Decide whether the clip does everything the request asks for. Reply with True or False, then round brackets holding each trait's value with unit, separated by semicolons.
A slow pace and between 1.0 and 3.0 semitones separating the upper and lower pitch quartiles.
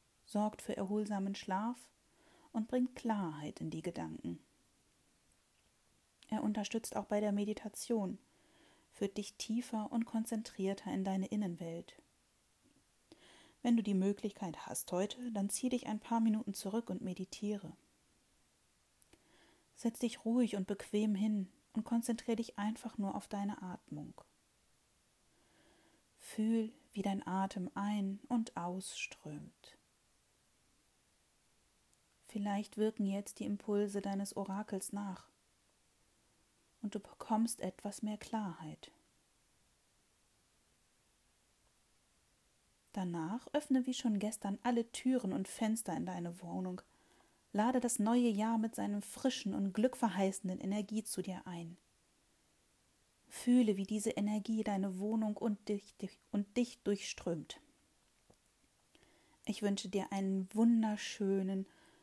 True (110 wpm; 2.7 semitones)